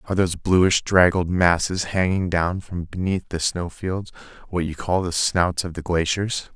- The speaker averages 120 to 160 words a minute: No, average, 185 wpm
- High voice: No, very low, 90 Hz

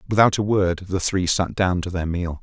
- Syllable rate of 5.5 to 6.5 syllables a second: No, 5.0 syllables/s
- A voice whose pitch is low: Yes, very low, 95 Hz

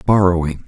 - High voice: No, very low, 90 Hz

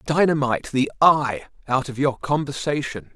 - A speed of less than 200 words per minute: Yes, slow, 135 wpm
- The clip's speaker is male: Yes, male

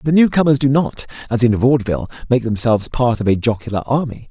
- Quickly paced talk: No, average, 195 wpm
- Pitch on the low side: Yes, low, 125 Hz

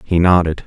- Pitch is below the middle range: Yes, very low, 85 Hz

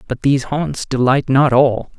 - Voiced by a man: Yes, male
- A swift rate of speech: No, average, 180 wpm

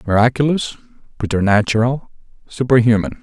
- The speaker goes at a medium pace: No, slow, 55 wpm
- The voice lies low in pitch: Yes, low, 120 Hz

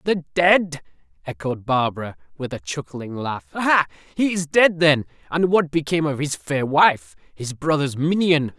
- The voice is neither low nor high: Yes, medium, 150 Hz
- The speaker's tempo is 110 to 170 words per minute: Yes, average, 160 wpm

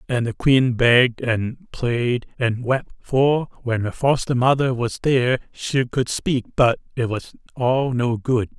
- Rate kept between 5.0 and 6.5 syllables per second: No, 3.8 syllables/s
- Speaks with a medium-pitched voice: No, low, 125 Hz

